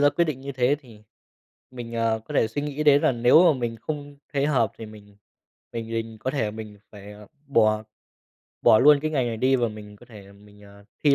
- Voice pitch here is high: No, low, 115 Hz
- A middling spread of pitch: Yes, average, 4.5 semitones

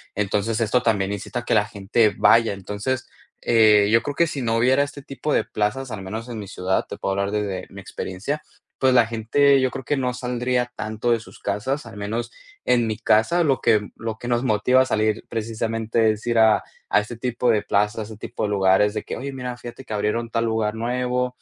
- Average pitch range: Yes, average, 3.0 semitones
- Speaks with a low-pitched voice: Yes, low, 115 Hz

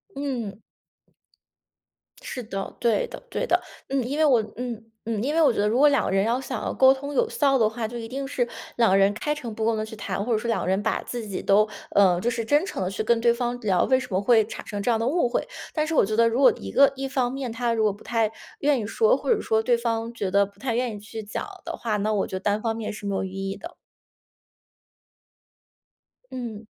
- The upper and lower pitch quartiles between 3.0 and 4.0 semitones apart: Yes, average, 3.4 semitones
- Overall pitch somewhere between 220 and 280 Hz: Yes, high, 230 Hz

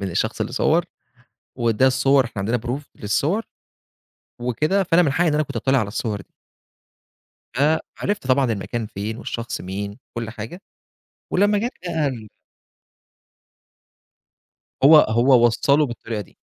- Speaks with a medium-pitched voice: No, low, 125 Hz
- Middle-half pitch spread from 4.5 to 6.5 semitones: Yes, average, 5.1 semitones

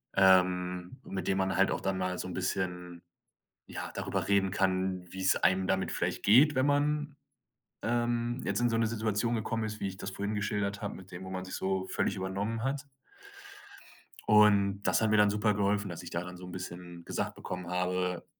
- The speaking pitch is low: Yes, very low, 95 Hz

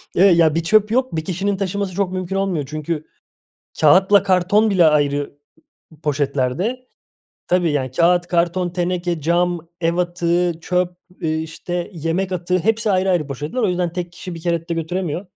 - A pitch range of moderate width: No, narrow, 2.3 semitones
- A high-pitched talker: No, medium, 175 Hz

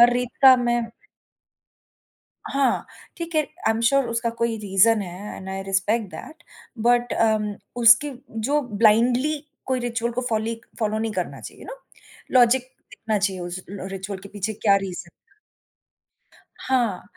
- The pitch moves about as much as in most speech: Yes, average, 3.3 semitones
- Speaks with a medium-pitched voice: No, high, 230 Hz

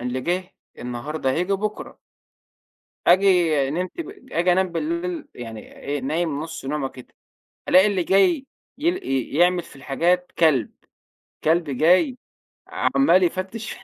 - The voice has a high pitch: No, medium, 175 Hz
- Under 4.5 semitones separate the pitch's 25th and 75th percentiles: No, average, 4.8 semitones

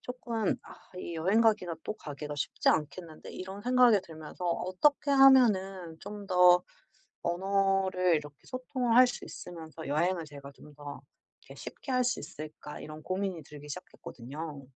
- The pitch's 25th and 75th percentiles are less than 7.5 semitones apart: Yes, wide, 5.5 semitones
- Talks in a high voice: No, medium, 180 Hz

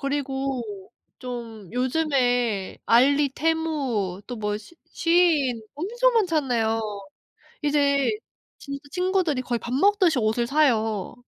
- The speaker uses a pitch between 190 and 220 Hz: No, very high, 270 Hz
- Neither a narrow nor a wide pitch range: Yes, average, 5.0 semitones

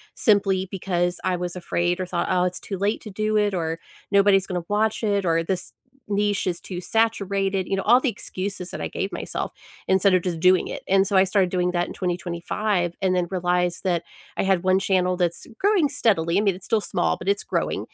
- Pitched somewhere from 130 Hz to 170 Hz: No, high, 190 Hz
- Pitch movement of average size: No, narrow, 2.2 semitones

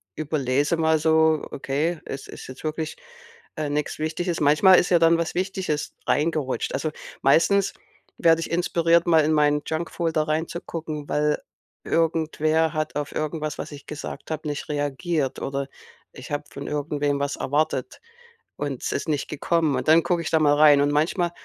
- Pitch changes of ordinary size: No, narrow, 2.1 semitones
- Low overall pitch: No, medium, 155 Hz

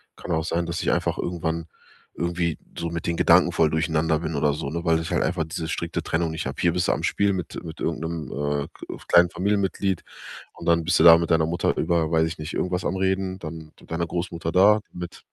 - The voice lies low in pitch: Yes, very low, 85 Hz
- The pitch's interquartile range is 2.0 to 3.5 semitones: No, narrow, 1.5 semitones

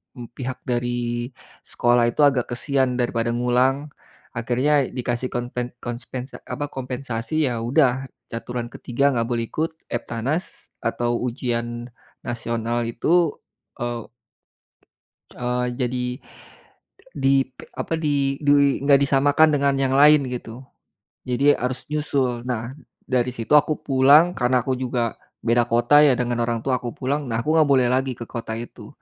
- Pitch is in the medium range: No, low, 125 Hz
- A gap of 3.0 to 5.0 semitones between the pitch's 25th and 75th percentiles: No, narrow, 2.6 semitones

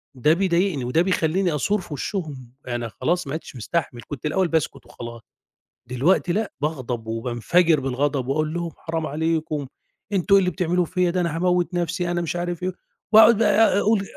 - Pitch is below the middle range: No, medium, 165 Hz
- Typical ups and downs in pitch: Yes, average, 4.5 semitones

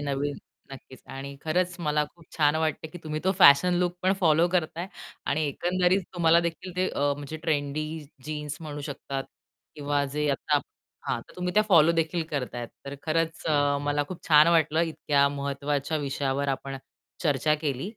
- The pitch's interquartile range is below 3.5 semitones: Yes, average, 2.8 semitones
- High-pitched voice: No, medium, 150 Hz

